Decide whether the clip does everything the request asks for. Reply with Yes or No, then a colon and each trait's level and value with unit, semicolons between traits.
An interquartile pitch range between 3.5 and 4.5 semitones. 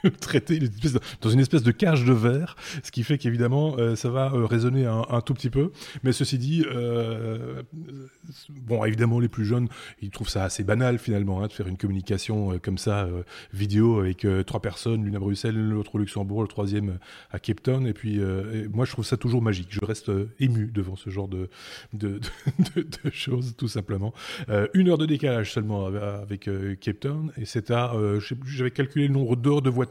Yes: average, 4.2 semitones